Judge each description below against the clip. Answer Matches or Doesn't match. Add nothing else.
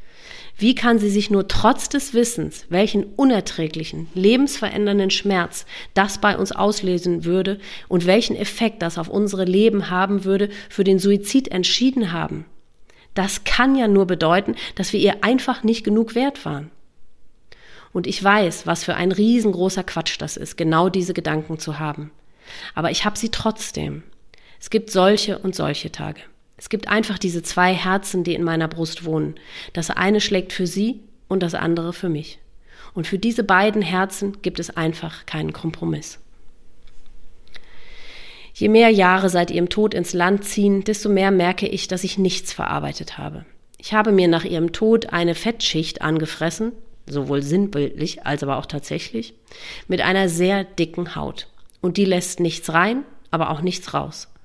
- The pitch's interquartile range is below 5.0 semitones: Matches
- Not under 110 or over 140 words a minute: Doesn't match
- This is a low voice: Doesn't match